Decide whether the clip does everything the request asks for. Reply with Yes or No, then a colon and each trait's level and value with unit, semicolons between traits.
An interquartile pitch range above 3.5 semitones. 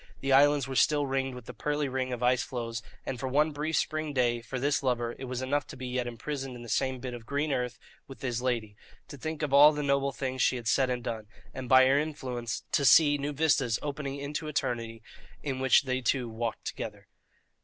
No: average, 2.7 semitones